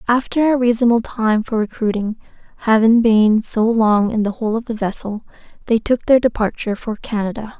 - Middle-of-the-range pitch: No, high, 225 Hz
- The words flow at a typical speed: Yes, average, 175 wpm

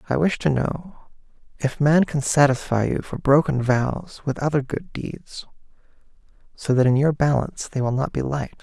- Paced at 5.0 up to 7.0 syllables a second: No, 4.7 syllables/s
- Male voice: Yes, male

